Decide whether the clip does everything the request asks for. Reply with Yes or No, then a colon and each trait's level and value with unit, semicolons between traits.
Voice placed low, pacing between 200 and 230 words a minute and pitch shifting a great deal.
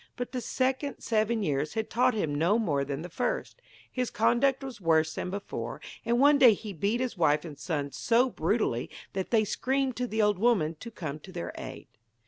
No: high, 215 Hz; fast, 205 wpm; wide, 7.3 semitones